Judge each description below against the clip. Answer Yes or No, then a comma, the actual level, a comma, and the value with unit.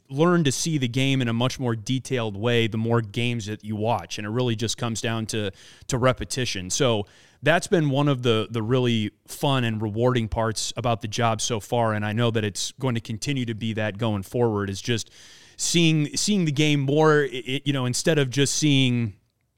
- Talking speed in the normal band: No, fast, 220 wpm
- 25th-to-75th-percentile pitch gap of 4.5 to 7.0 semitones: No, average, 3.2 semitones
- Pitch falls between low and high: No, low, 120 Hz